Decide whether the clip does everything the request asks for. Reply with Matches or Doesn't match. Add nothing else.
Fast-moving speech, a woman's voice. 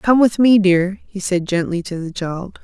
Matches